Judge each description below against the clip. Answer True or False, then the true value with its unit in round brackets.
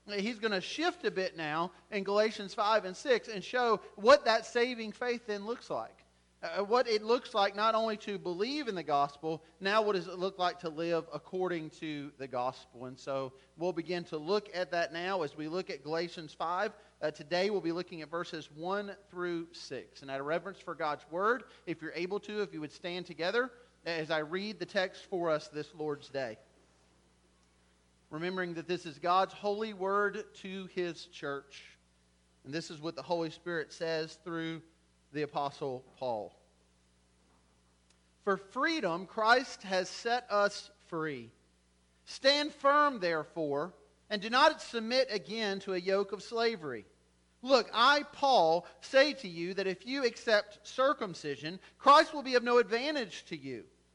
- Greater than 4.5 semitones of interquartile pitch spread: True (5.5 semitones)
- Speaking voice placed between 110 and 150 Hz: False (180 Hz)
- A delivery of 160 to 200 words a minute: True (175 wpm)